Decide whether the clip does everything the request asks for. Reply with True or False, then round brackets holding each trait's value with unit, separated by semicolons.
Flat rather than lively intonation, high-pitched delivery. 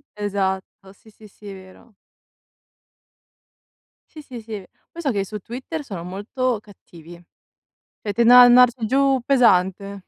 False (4.3 semitones; 215 Hz)